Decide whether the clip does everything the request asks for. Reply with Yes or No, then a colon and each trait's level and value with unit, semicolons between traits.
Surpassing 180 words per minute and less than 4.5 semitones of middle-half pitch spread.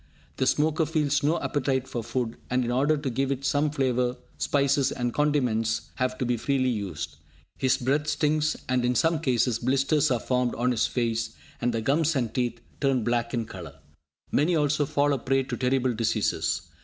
Yes: average, 190 wpm; average, 3.2 semitones